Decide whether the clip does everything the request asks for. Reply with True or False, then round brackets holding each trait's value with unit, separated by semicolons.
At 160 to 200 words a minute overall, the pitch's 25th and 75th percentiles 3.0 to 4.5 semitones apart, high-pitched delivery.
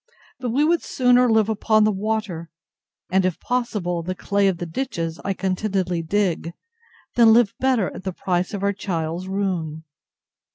True (165 wpm; 3.8 semitones; 195 Hz)